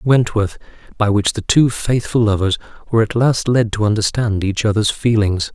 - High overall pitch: No, low, 110 Hz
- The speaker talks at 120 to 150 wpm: No, average, 175 wpm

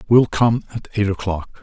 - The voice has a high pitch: No, low, 105 Hz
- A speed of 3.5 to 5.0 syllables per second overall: Yes, 4.8 syllables/s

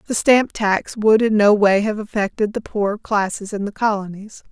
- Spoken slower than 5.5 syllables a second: Yes, 4.9 syllables/s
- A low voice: No, high, 210 Hz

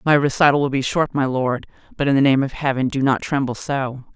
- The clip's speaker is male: No, female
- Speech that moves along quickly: Yes, fast, 245 wpm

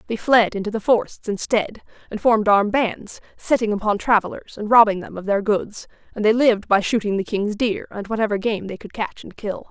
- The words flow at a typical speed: No, fast, 215 wpm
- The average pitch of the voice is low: No, high, 210 Hz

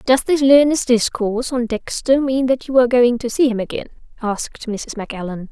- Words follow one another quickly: No, average, 195 wpm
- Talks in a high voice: Yes, high, 245 Hz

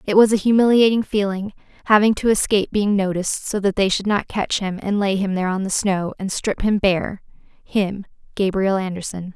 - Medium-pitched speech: No, high, 200 Hz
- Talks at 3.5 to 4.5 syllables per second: No, 5.3 syllables/s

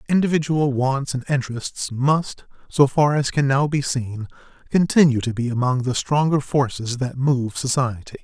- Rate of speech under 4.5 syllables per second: No, 4.7 syllables/s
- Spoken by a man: Yes, male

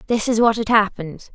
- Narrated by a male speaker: No, female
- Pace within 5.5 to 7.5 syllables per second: Yes, 6.0 syllables/s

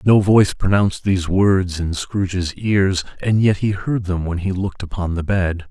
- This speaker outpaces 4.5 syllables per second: Yes, 4.8 syllables/s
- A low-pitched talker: Yes, very low, 95 Hz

